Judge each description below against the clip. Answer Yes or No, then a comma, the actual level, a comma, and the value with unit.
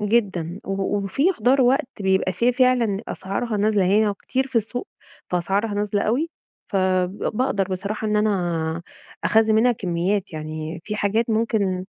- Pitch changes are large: No, average, 3.4 semitones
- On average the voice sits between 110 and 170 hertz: No, high, 205 Hz